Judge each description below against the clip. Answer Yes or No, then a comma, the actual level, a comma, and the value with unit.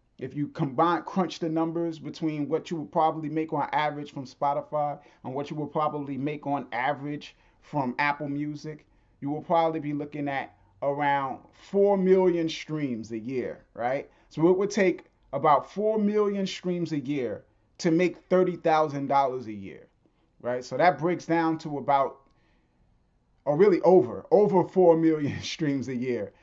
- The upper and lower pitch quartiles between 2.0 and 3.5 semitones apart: Yes, average, 3.0 semitones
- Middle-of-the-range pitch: Yes, medium, 150 Hz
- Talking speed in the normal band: Yes, average, 165 wpm